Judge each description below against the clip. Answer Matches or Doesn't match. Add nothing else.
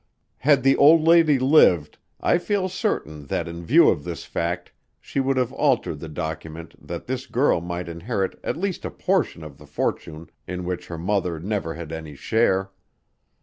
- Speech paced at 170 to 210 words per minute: Matches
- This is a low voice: Matches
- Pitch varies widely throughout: Matches